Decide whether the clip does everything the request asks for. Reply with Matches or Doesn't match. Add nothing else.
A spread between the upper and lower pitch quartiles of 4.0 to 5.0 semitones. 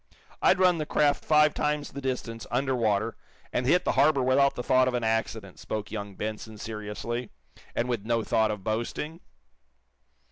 Matches